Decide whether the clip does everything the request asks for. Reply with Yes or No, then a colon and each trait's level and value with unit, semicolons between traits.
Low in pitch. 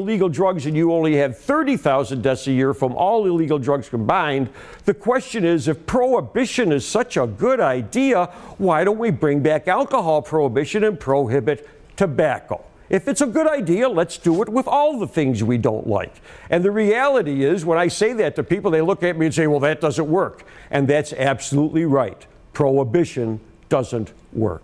No: medium, 160 Hz